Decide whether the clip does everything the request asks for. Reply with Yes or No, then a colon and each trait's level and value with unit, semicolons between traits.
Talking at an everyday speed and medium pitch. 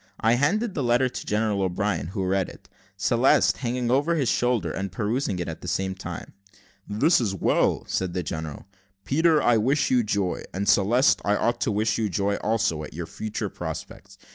No: average, 190 wpm; low, 105 Hz